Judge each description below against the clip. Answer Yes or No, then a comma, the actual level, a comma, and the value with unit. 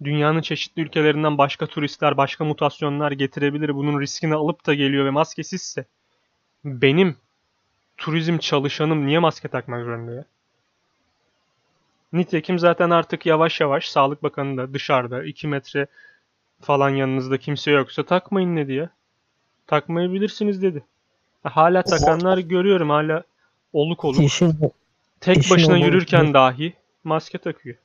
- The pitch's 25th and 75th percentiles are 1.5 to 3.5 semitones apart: Yes, average, 3.1 semitones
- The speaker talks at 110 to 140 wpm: Yes, average, 120 wpm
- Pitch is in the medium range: Yes, medium, 150 Hz